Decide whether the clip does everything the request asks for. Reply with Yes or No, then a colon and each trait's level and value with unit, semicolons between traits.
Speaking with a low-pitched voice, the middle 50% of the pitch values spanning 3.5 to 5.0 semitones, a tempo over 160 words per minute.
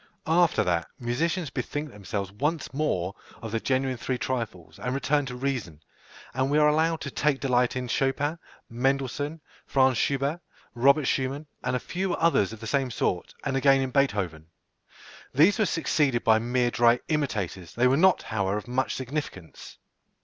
Yes: low, 130 Hz; average, 4.1 semitones; average, 170 wpm